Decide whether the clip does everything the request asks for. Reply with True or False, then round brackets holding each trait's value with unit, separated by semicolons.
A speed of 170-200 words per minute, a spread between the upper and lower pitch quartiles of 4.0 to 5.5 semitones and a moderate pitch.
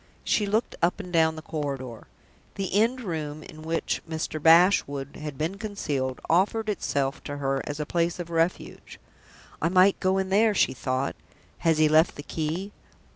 True (175 wpm; 4.4 semitones; 165 Hz)